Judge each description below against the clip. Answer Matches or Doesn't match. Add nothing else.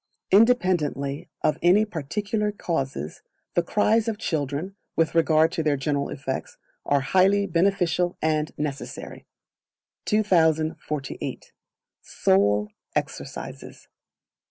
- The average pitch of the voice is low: Doesn't match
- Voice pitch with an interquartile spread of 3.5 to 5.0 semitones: Doesn't match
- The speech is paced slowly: Matches